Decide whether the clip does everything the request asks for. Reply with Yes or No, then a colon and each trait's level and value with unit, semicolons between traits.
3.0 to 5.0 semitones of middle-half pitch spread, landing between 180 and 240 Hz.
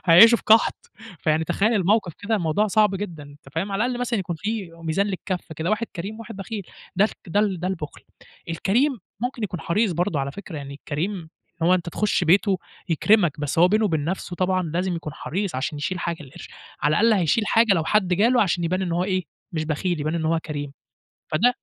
Yes: average, 4.4 semitones; medium, 185 Hz